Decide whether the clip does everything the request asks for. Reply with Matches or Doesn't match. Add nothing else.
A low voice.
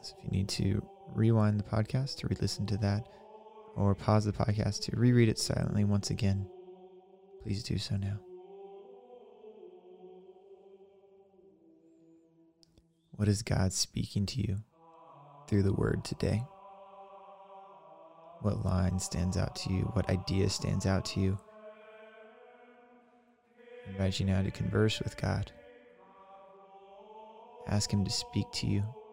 Doesn't match